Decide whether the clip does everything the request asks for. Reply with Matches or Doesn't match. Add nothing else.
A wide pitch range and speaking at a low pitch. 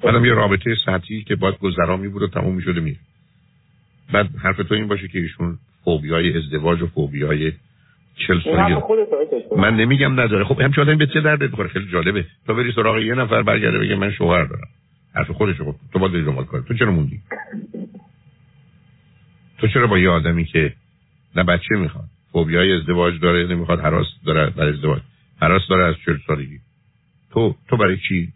Matches